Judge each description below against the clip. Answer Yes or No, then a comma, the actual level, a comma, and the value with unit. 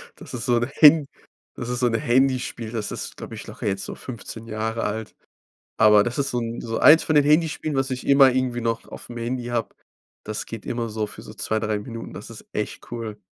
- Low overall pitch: Yes, low, 120 Hz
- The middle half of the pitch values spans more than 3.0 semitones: No, narrow, 2.5 semitones